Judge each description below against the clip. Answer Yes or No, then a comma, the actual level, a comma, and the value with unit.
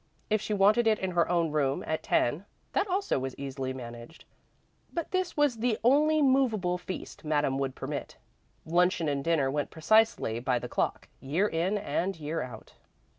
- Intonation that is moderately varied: No, wide, 7.9 semitones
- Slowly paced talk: No, average, 175 wpm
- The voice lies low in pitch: No, medium, 170 Hz